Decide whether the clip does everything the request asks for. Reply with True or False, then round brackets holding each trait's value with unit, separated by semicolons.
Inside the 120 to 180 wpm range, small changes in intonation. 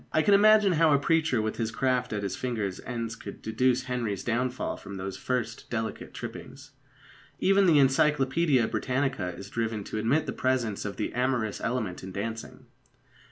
False (170 wpm; 3.7 semitones)